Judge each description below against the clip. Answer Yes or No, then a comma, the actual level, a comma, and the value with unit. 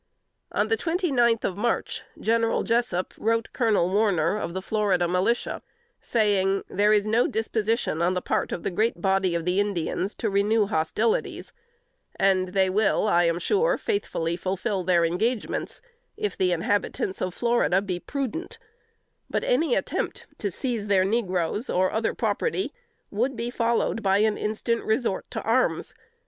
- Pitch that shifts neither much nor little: Yes, average, 3.9 semitones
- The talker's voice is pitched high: Yes, high, 210 Hz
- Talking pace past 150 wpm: Yes, average, 160 wpm